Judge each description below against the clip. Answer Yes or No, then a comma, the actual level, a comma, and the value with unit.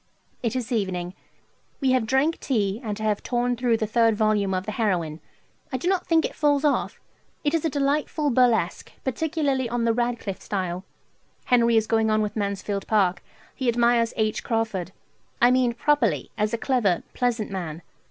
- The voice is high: Yes, high, 230 Hz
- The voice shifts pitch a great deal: No, average, 3.8 semitones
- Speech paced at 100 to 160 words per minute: No, average, 180 wpm